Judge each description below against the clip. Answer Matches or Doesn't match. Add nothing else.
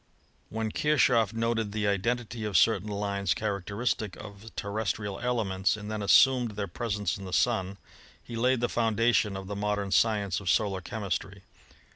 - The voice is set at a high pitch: Doesn't match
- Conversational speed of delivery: Matches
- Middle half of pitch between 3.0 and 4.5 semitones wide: Doesn't match